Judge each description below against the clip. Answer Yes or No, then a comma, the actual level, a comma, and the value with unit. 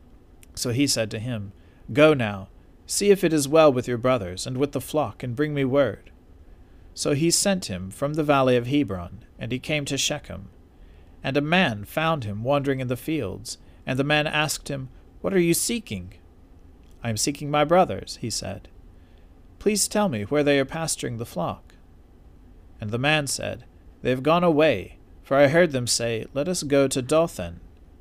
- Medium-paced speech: Yes, average, 190 wpm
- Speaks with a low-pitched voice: Yes, low, 125 Hz